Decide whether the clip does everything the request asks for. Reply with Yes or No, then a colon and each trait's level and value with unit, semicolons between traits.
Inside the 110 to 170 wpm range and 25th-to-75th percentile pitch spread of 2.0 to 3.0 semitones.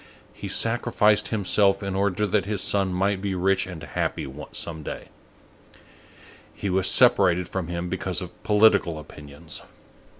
Yes: average, 140 wpm; narrow, 2.6 semitones